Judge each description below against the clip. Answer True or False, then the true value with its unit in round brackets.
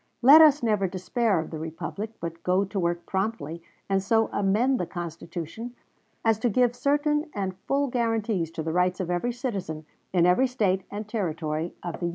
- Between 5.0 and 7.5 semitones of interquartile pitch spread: True (5.5 semitones)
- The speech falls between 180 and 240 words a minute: True (190 wpm)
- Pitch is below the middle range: False (195 Hz)